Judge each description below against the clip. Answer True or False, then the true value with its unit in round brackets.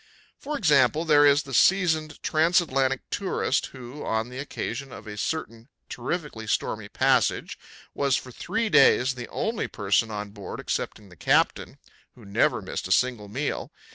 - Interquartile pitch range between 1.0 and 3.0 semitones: False (5.5 semitones)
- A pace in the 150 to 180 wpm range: True (160 wpm)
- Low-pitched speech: True (130 Hz)